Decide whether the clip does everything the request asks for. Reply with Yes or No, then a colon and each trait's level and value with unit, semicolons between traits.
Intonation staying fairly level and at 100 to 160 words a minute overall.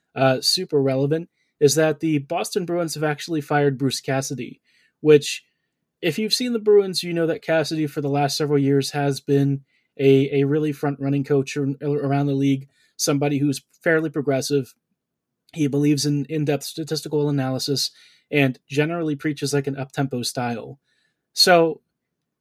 Yes: narrow, 2.2 semitones; average, 155 wpm